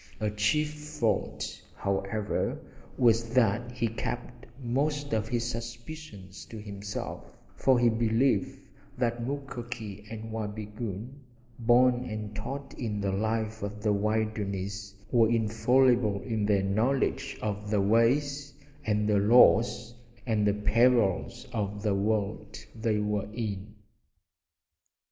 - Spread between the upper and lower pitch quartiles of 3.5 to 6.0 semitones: No, average, 2.7 semitones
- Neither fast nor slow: No, slow, 120 wpm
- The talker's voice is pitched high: No, low, 110 Hz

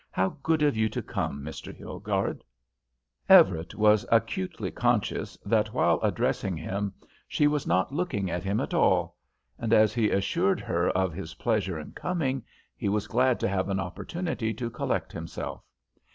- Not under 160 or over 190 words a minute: Yes, average, 165 wpm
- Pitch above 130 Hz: No, low, 105 Hz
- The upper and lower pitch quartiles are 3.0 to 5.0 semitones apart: No, wide, 5.4 semitones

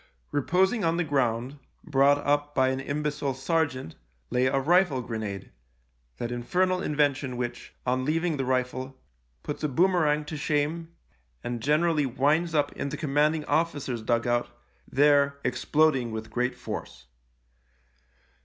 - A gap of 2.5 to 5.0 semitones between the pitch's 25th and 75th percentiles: Yes, average, 3.4 semitones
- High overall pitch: No, medium, 140 Hz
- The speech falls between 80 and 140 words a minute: Yes, slow, 135 wpm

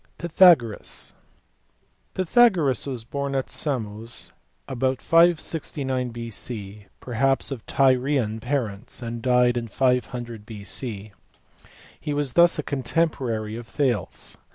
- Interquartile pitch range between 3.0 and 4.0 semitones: Yes, average, 3.7 semitones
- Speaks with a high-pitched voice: No, low, 125 Hz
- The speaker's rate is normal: No, slow, 105 wpm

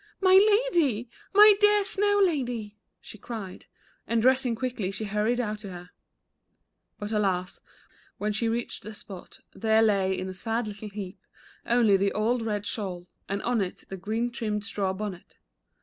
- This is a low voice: No, high, 215 Hz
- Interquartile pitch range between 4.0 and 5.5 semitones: No, average, 3.5 semitones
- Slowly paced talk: No, average, 165 wpm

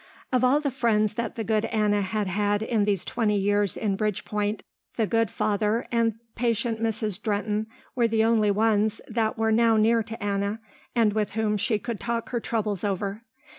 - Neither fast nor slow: Yes, average, 185 wpm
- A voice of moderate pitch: No, high, 215 Hz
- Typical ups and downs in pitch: No, narrow, 1.7 semitones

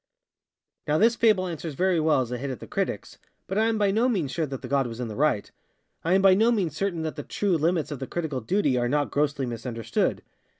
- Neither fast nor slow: No, fast, 245 wpm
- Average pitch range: No, wide, 6.2 semitones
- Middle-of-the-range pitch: Yes, medium, 155 Hz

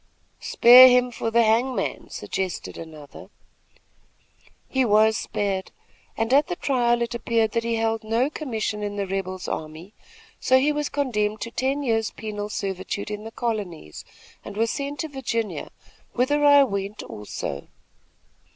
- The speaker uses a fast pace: No, average, 150 wpm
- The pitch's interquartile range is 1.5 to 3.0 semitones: No, average, 3.8 semitones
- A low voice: No, high, 225 Hz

